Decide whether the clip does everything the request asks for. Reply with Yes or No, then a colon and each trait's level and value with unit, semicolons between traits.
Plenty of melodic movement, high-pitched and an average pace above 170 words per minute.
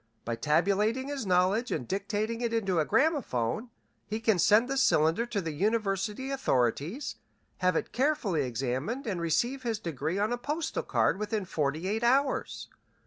No: wide, 6.6 semitones; high, 210 Hz; average, 160 wpm